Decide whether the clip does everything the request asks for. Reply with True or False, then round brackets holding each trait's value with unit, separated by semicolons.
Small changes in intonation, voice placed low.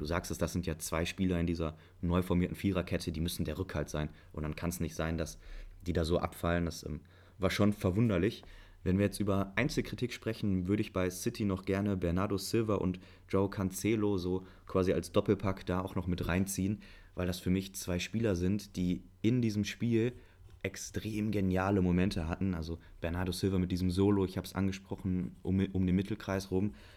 True (2.2 semitones; 95 Hz)